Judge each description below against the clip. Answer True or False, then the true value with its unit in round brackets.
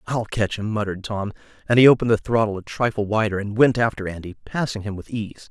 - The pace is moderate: False (230 wpm)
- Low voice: True (110 Hz)